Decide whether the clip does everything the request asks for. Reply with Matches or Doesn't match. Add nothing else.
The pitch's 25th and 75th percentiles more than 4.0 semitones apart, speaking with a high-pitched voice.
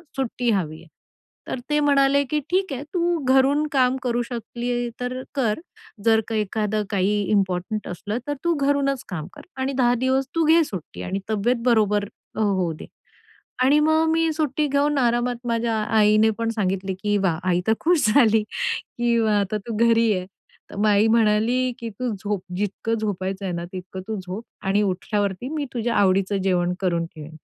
Matches